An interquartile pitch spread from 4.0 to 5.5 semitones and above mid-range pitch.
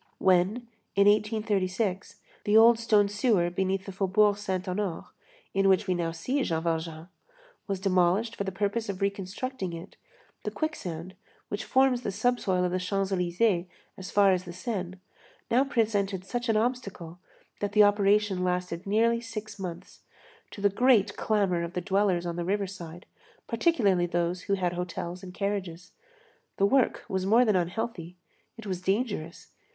No: average, 2.8 semitones; high, 195 Hz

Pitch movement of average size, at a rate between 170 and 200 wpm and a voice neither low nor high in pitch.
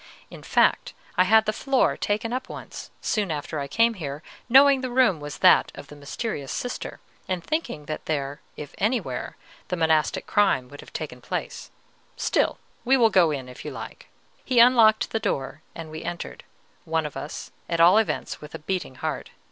No: wide, 7.4 semitones; average, 190 wpm; medium, 180 Hz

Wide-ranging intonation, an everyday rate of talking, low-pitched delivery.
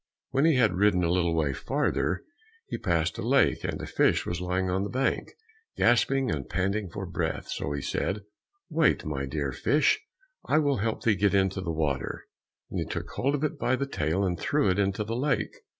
No: wide, 7.0 semitones; fast, 215 wpm; low, 100 Hz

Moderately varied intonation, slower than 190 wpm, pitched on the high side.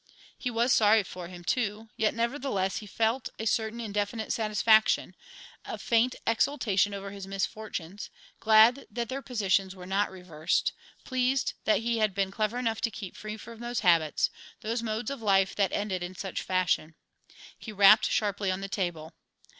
Yes: average, 3.0 semitones; average, 170 wpm; high, 215 Hz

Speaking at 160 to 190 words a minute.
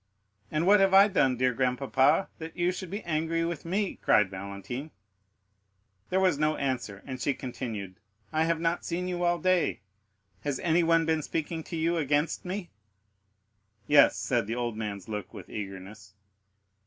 Yes: average, 165 wpm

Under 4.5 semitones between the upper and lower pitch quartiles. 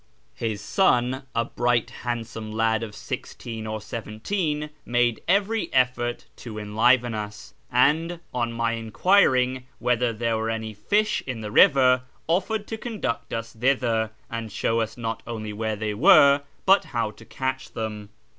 Yes: average, 3.0 semitones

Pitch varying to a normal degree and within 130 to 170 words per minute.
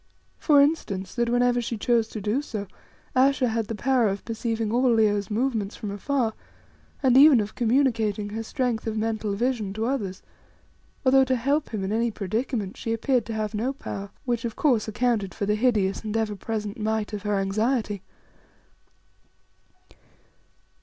Yes: average, 3.0 semitones; average, 165 wpm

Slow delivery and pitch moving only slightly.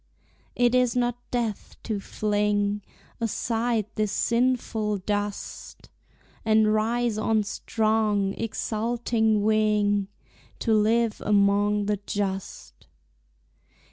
Yes: slow, 90 wpm; narrow, 1.9 semitones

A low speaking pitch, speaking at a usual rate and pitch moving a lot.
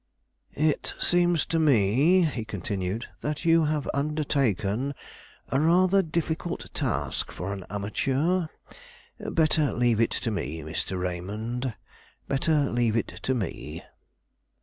No: low, 130 Hz; slow, 120 wpm; wide, 7.4 semitones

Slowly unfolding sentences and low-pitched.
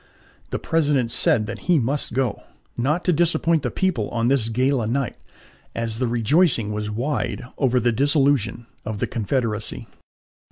No: average, 155 wpm; low, 125 Hz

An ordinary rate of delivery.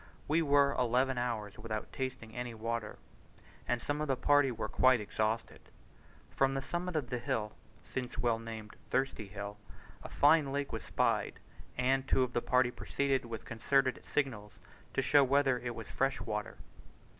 Yes: average, 165 wpm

